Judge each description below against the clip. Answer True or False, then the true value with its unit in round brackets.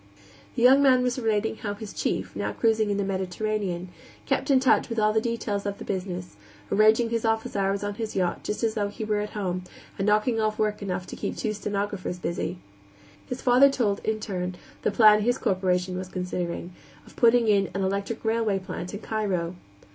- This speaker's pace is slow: False (200 wpm)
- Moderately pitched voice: False (210 Hz)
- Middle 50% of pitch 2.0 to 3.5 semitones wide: True (2.7 semitones)